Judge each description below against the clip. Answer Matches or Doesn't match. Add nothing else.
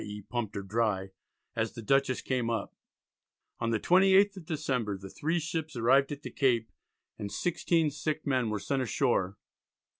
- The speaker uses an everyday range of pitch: Doesn't match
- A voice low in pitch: Matches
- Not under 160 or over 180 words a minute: Matches